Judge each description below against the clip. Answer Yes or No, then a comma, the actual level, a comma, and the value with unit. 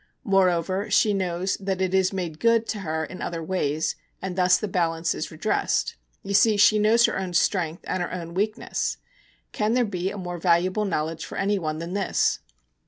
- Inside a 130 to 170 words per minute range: No, average, 190 wpm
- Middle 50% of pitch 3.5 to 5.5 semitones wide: No, average, 2.8 semitones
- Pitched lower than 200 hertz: Yes, medium, 185 Hz